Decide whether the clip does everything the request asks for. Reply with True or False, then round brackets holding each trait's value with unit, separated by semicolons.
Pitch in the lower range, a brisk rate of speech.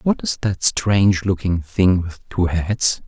False (95 Hz; 175 wpm)